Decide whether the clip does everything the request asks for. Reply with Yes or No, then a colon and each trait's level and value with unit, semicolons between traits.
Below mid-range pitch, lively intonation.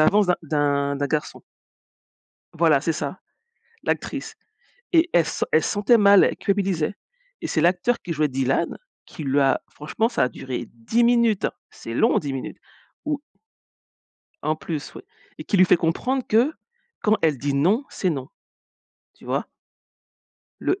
No: medium, 165 Hz; wide, 6.5 semitones